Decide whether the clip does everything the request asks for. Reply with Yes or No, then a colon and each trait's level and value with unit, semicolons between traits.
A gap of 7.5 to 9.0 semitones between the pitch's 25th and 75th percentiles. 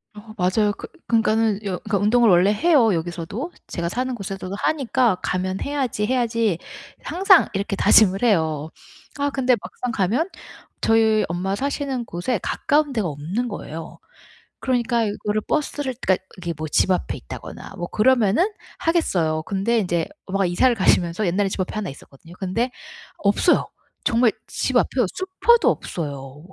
No: wide, 5.4 semitones